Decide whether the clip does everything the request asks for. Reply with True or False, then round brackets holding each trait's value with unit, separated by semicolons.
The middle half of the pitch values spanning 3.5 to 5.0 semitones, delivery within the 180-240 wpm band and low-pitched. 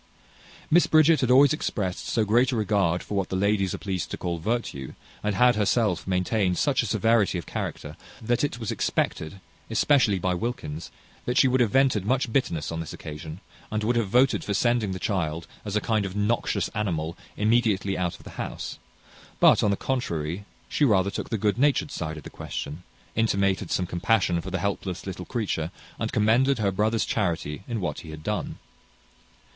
True (4.6 semitones; 195 wpm; 100 Hz)